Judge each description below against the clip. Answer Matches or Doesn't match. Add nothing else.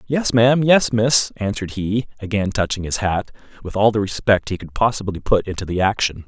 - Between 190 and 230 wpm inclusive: Matches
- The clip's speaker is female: Doesn't match